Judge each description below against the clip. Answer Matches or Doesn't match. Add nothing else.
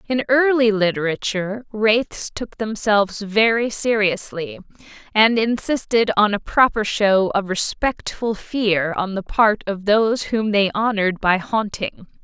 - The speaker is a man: Doesn't match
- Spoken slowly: Matches